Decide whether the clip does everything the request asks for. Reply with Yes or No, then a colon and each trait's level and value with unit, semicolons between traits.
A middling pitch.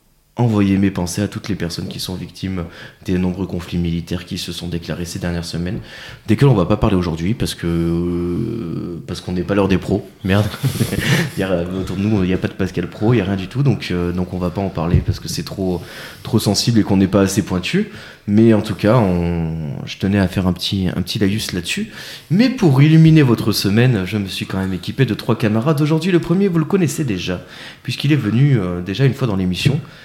No: low, 100 Hz